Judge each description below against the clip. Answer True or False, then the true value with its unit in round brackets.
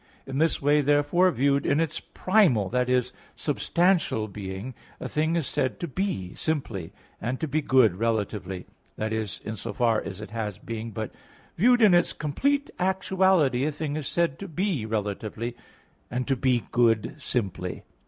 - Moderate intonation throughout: False (6.7 semitones)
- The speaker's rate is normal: True (165 wpm)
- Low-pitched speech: True (130 Hz)